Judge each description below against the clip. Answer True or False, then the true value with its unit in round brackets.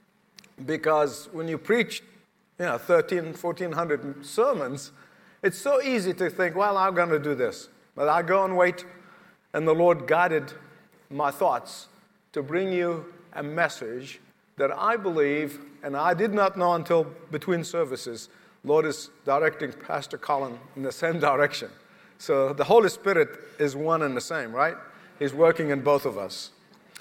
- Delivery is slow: False (160 wpm)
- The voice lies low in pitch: False (170 Hz)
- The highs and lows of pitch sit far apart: False (4.1 semitones)